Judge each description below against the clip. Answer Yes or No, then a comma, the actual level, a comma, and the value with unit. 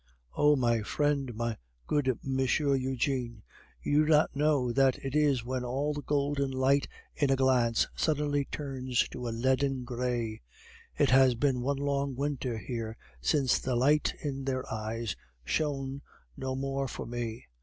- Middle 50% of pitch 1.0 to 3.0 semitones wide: Yes, narrow, 2.5 semitones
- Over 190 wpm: No, average, 155 wpm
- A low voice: Yes, low, 130 Hz